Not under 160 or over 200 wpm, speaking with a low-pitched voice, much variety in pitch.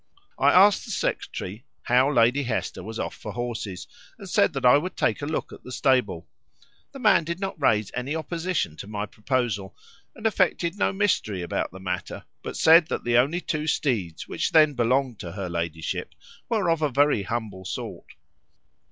Yes: average, 185 wpm; low, 125 Hz; wide, 7.7 semitones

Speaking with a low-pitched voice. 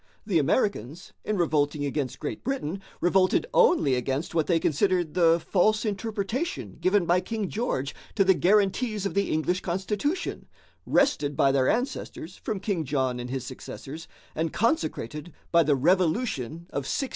No: medium, 175 Hz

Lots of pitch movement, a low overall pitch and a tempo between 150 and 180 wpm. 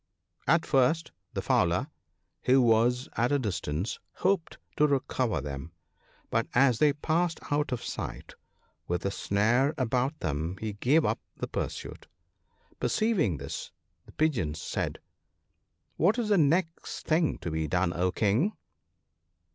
No: wide, 8.6 semitones; low, 125 Hz; average, 140 wpm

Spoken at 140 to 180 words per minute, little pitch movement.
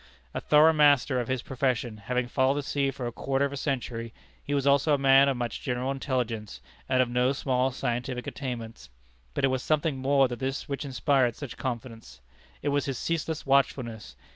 No: average, 195 wpm; narrow, 2.3 semitones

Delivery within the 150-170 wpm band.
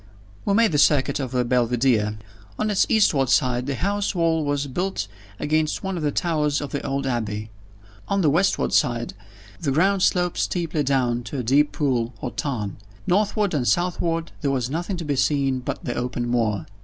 No: average, 190 wpm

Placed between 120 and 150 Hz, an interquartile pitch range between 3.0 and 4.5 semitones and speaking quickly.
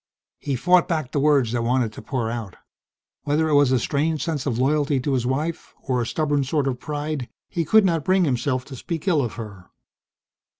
Yes: medium, 140 Hz; average, 3.7 semitones; fast, 210 wpm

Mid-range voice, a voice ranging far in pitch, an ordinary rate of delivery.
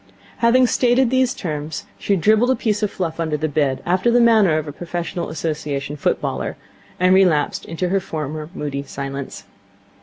Yes: medium, 170 Hz; wide, 6.1 semitones; average, 170 wpm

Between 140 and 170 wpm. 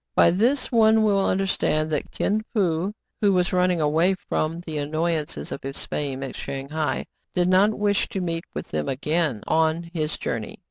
No: average, 180 wpm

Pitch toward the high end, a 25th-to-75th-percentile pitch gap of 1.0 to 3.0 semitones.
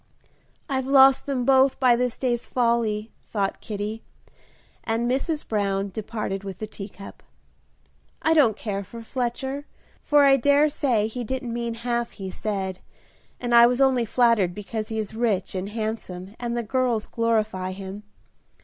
No: high, 230 Hz; average, 3.4 semitones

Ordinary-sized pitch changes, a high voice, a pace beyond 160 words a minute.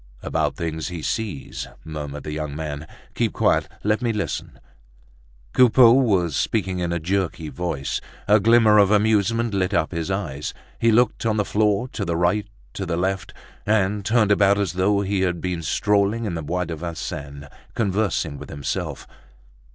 No: average, 4.2 semitones; very low, 95 Hz; average, 170 wpm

